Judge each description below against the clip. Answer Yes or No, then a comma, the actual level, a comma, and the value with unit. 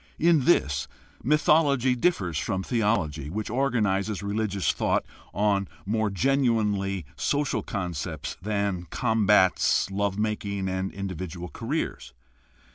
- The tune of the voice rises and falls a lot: No, average, 3.5 semitones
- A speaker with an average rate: No, slow, 105 wpm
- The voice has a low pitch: Yes, low, 100 Hz